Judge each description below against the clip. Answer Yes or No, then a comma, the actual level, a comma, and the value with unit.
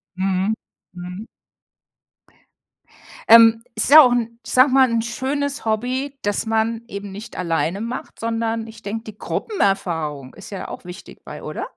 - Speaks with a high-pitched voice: Yes, high, 225 Hz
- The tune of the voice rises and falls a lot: No, average, 3.2 semitones